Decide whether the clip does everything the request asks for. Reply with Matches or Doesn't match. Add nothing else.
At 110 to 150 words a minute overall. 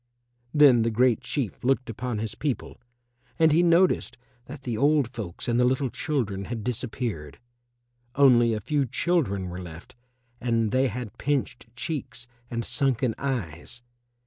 Matches